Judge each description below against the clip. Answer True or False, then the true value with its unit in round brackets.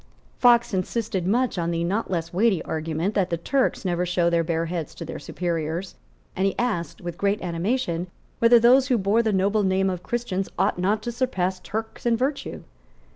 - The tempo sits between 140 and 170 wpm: False (190 wpm)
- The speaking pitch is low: False (190 Hz)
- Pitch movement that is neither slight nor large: True (4.9 semitones)